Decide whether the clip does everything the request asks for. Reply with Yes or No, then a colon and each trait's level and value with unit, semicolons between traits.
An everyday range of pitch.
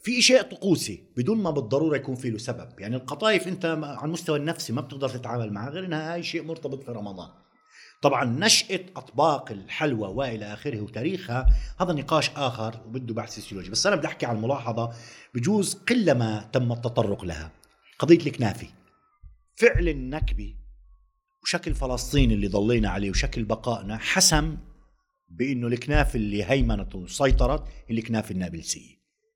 No: wide, 6.3 semitones